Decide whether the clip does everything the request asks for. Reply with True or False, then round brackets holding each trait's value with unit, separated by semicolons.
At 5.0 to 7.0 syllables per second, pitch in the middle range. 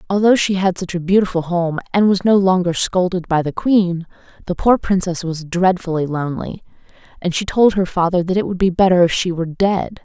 True (5.5 syllables/s; 180 Hz)